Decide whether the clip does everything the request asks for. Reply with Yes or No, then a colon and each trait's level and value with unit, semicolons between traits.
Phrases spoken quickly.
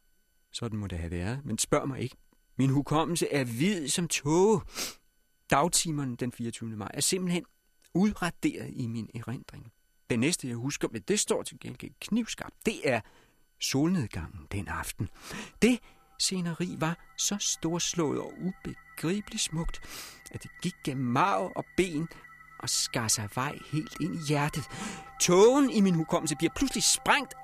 No: average, 155 wpm